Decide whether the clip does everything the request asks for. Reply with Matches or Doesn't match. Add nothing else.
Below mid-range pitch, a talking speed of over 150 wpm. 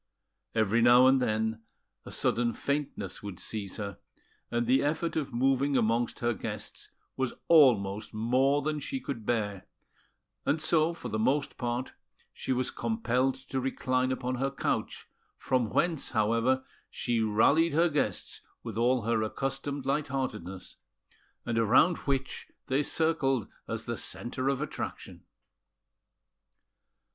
Doesn't match